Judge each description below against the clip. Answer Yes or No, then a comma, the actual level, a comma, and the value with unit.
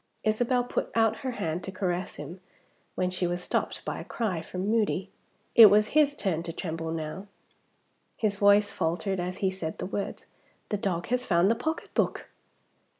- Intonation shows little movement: No, average, 3.6 semitones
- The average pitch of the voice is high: Yes, high, 195 Hz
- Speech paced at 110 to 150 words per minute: No, average, 175 wpm